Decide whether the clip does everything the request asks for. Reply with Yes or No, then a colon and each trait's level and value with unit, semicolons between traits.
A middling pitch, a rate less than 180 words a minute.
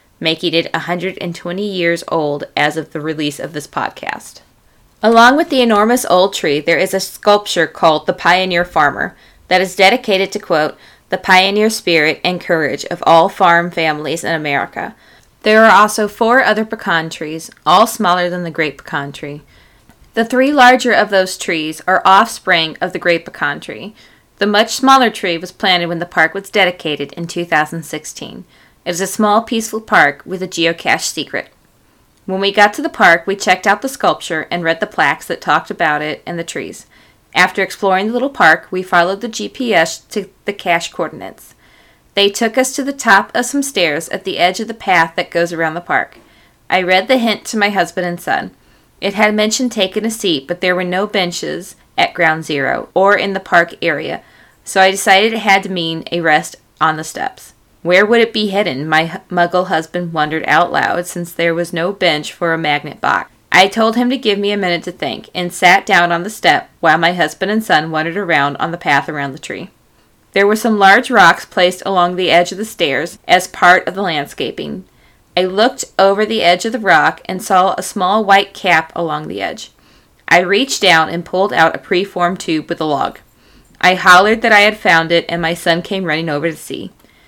No: medium, 180 Hz; fast, 205 wpm